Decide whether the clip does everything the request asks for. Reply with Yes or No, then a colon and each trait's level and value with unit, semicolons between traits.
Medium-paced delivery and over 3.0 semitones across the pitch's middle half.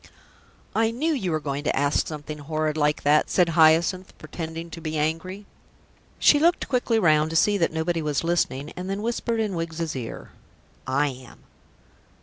Yes: average, 170 wpm; average, 3.7 semitones